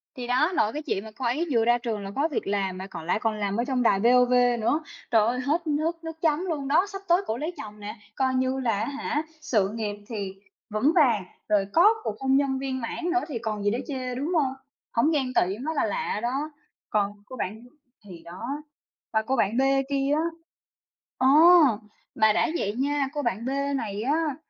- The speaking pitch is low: No, very high, 250 Hz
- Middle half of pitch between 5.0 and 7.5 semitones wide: Yes, average, 5.3 semitones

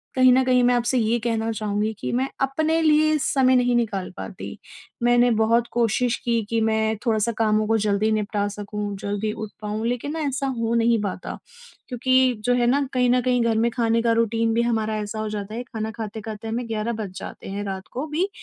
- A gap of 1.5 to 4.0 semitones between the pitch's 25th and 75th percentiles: Yes, narrow, 2.4 semitones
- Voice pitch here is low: No, high, 230 Hz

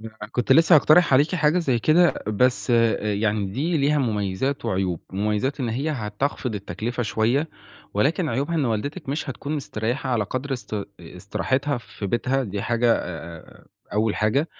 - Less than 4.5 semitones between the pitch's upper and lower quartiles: No, average, 5.1 semitones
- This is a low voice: Yes, low, 120 Hz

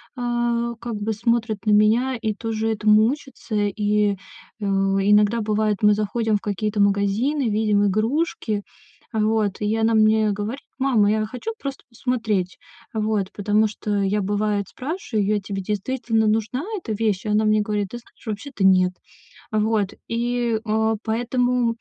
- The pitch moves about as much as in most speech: No, narrow, 2.1 semitones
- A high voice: Yes, high, 215 Hz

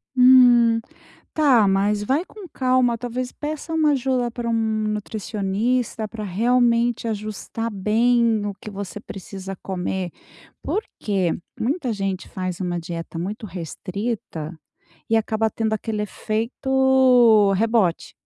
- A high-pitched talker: Yes, high, 220 Hz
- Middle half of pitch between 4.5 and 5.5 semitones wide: No, average, 3.7 semitones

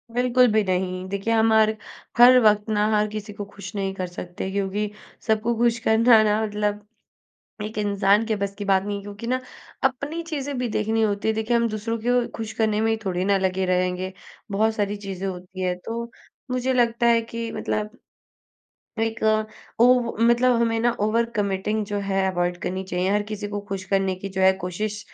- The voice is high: Yes, high, 210 Hz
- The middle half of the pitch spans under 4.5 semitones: Yes, average, 2.8 semitones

